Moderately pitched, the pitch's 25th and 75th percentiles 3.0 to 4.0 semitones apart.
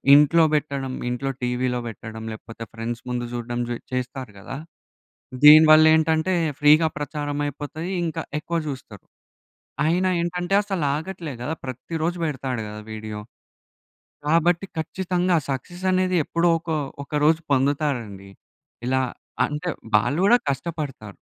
No: medium, 145 Hz; average, 5.1 semitones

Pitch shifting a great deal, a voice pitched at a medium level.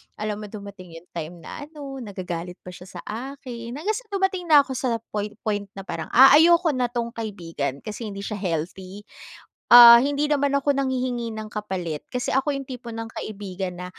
No: wide, 6.0 semitones; high, 225 Hz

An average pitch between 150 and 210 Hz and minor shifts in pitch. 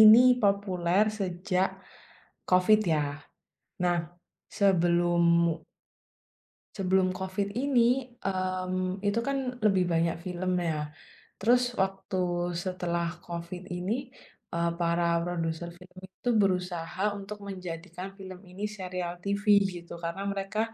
Yes: medium, 185 Hz; narrow, 2.1 semitones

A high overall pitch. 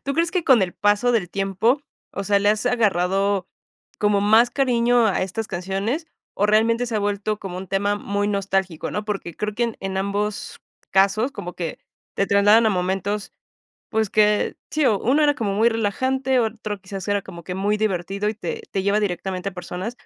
Yes: high, 205 Hz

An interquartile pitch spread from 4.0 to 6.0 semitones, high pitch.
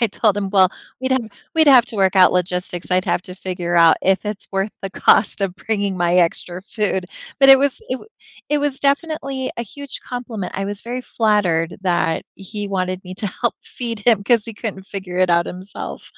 Yes: average, 4.5 semitones; high, 200 Hz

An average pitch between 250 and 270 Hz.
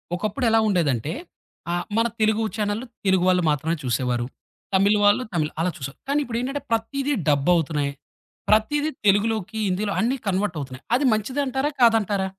No: high, 205 Hz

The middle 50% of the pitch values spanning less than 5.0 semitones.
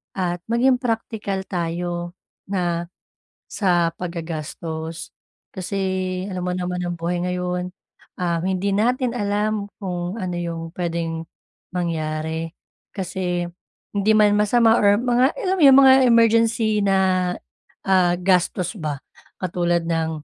Yes: average, 3.4 semitones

